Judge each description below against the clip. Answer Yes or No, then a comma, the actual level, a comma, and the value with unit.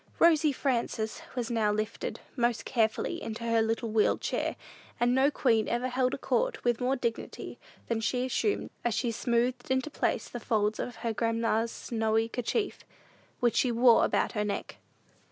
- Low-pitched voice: No, high, 235 Hz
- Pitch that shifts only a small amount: Yes, narrow, 2.2 semitones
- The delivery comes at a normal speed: Yes, average, 170 wpm